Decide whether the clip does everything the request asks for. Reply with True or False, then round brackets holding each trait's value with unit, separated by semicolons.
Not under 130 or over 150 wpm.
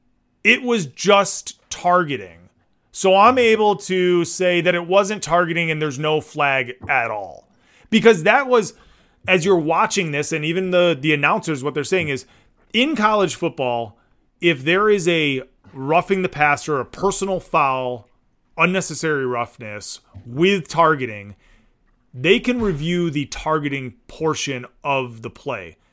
True (140 wpm)